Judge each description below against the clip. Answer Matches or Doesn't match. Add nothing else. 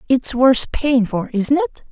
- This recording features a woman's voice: Matches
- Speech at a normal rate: Matches